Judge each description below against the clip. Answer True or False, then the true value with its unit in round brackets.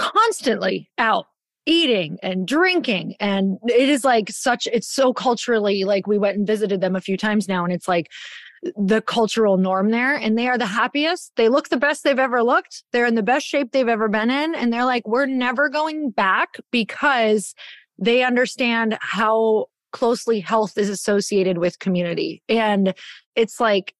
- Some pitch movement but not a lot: True (3.9 semitones)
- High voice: True (230 Hz)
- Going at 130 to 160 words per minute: False (180 wpm)